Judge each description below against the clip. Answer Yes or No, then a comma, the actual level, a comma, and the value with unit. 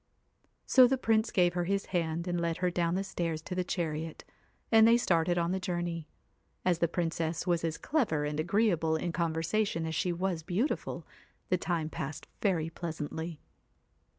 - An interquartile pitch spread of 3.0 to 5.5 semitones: No, narrow, 2.4 semitones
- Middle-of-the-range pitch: Yes, medium, 175 Hz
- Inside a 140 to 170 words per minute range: No, average, 180 wpm